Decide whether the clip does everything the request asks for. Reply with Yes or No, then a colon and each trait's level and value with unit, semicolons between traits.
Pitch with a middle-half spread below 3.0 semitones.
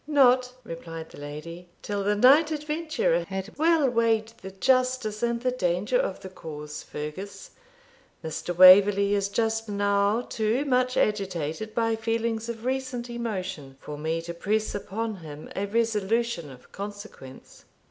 No: average, 4.7 semitones